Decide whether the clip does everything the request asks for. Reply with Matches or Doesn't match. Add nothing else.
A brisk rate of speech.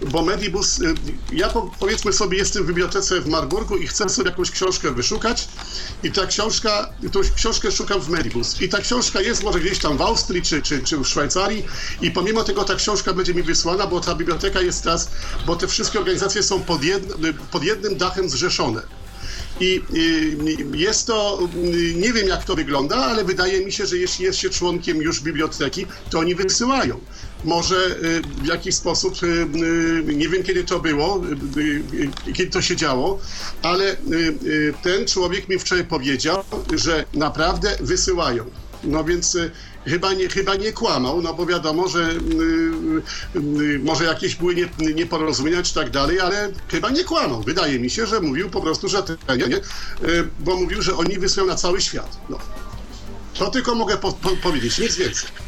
Matches